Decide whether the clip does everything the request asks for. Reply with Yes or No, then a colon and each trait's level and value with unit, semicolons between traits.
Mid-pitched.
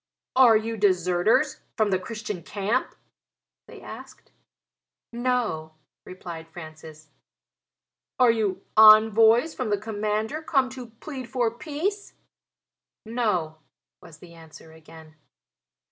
No: high, 215 Hz